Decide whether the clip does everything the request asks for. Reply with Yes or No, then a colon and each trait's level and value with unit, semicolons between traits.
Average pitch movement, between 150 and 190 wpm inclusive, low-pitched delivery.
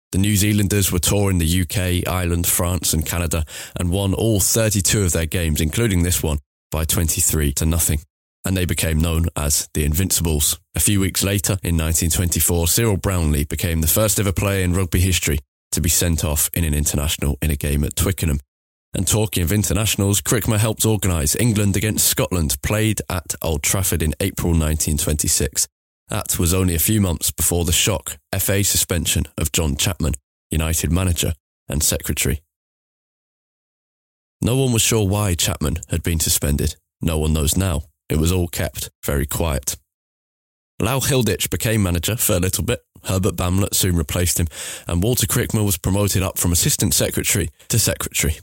Yes: average, 4.0 semitones; average, 170 wpm; very low, 90 Hz